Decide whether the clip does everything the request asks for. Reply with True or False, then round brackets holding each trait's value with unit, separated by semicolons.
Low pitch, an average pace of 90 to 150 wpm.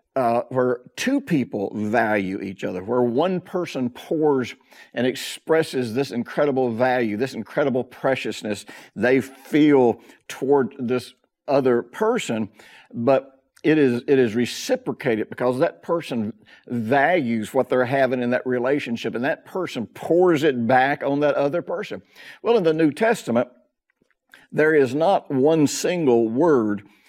True (130 Hz; 135 wpm)